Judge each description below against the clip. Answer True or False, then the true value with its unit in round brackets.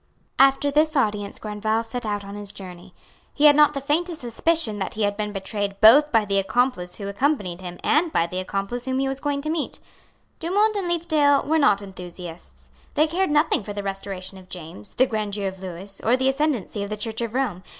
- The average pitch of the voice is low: False (215 Hz)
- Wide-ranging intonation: True (6.5 semitones)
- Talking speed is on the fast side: True (210 wpm)